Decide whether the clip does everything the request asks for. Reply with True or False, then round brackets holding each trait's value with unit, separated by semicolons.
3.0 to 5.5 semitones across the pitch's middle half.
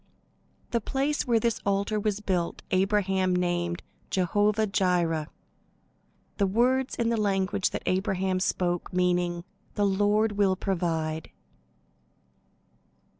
False (2.6 semitones)